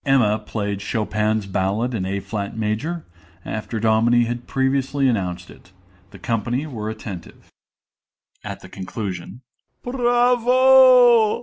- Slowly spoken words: Yes, slow, 125 wpm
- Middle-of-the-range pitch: No, low, 115 Hz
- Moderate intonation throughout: No, wide, 5.8 semitones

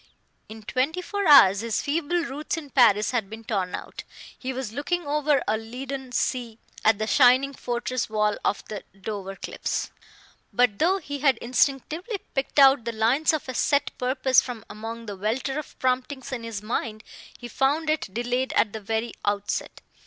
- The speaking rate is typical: Yes, average, 175 wpm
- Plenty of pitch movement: No, average, 4.1 semitones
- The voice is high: Yes, very high, 250 Hz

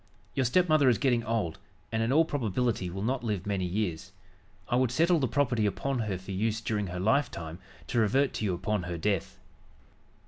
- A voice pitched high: No, low, 110 Hz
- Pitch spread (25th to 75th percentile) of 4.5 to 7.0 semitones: Yes, average, 5.2 semitones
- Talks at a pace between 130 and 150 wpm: No, average, 195 wpm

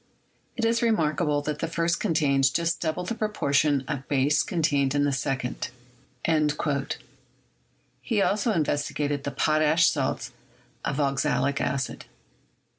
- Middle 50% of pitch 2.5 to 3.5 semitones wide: Yes, average, 3.2 semitones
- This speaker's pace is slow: Yes, slow, 120 wpm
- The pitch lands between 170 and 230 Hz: No, medium, 150 Hz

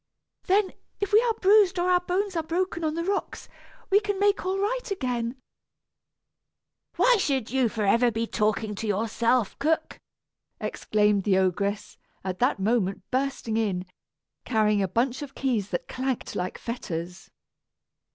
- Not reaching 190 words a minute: Yes, average, 150 wpm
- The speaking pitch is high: Yes, very high, 250 Hz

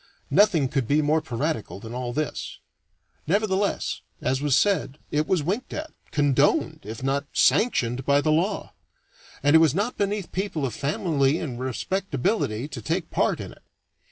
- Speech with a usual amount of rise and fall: No, wide, 6.1 semitones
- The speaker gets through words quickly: No, average, 160 wpm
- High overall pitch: No, medium, 150 Hz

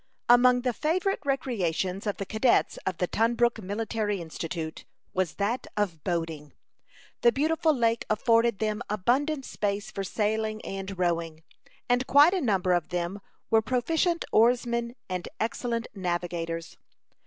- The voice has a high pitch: Yes, high, 215 Hz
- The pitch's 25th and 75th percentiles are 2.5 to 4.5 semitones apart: No, average, 5.0 semitones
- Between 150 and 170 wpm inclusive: No, slow, 135 wpm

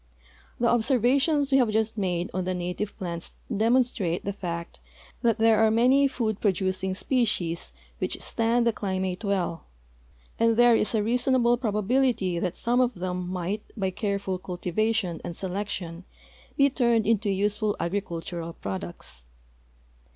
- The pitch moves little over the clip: No, average, 4.5 semitones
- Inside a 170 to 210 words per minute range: No, average, 145 wpm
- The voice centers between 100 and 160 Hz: No, high, 205 Hz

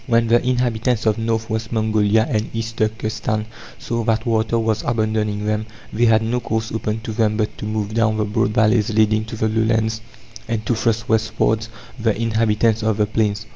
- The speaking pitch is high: No, low, 110 Hz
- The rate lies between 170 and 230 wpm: Yes, average, 190 wpm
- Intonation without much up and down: Yes, narrow, 1.0 semitones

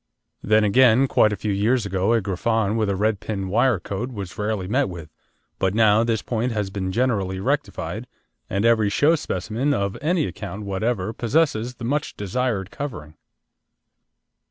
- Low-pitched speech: Yes, low, 110 Hz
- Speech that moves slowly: No, average, 165 wpm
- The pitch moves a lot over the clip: No, average, 3.8 semitones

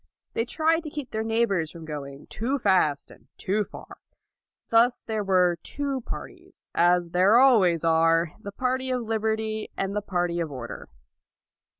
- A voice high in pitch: Yes, high, 200 Hz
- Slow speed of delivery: No, average, 170 wpm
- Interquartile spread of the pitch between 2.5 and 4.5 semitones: No, wide, 5.5 semitones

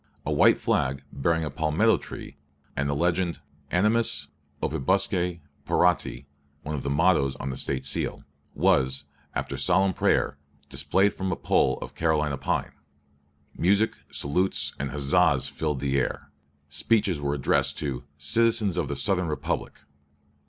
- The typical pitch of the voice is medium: No, very low, 80 Hz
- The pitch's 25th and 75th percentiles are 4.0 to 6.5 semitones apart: Yes, average, 4.8 semitones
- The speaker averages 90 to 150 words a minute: Yes, average, 140 wpm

